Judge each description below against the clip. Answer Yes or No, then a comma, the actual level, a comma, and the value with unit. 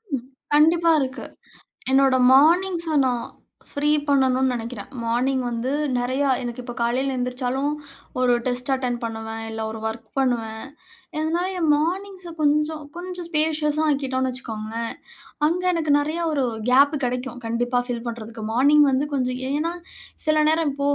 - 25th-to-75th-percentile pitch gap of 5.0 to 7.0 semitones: No, average, 3.8 semitones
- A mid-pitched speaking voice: No, very high, 265 Hz